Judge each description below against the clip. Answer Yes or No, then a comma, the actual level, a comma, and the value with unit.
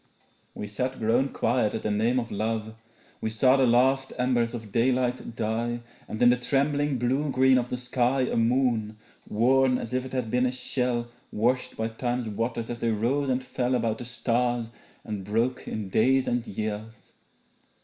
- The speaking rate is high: No, average, 180 wpm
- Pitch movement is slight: Yes, narrow, 2.2 semitones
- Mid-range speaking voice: No, low, 120 Hz